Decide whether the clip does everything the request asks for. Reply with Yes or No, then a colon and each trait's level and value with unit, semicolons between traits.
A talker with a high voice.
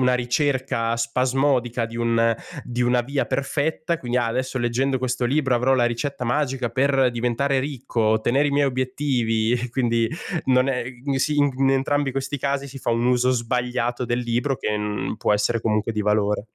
No: low, 125 Hz